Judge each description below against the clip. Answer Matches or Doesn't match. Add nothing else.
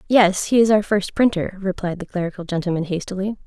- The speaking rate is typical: Matches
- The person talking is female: Matches